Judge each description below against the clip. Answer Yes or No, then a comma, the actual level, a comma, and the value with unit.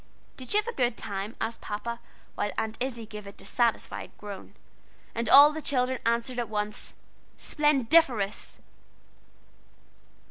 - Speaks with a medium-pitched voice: No, high, 235 Hz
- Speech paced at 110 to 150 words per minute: Yes, slow, 135 wpm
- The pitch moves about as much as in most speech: Yes, average, 3.7 semitones